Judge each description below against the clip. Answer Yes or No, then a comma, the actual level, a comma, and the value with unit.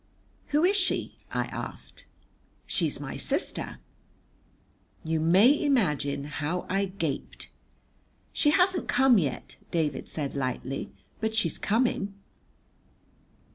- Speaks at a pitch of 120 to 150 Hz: No, high, 195 Hz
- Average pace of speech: No, slow, 105 wpm